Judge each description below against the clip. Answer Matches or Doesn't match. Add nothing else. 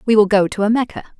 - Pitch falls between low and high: Doesn't match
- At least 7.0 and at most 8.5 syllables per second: Matches